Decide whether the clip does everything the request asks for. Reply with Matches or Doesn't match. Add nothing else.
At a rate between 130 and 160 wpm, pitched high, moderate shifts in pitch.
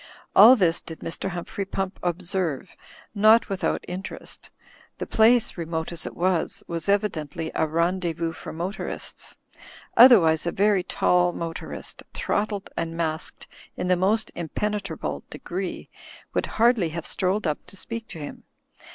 Doesn't match